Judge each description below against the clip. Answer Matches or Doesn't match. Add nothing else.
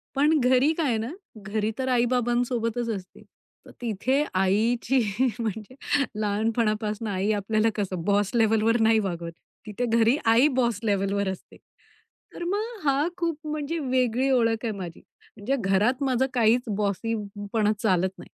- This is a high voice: Matches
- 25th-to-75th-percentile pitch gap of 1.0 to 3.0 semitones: Doesn't match